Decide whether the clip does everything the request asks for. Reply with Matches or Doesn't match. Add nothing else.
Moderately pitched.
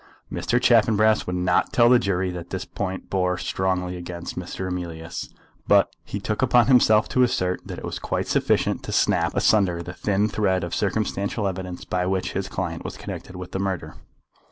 Doesn't match